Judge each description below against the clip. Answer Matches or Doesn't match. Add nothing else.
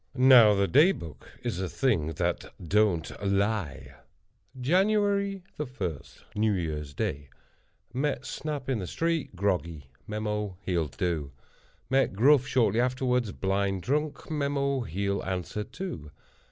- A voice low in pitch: Matches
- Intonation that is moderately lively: Doesn't match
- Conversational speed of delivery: Doesn't match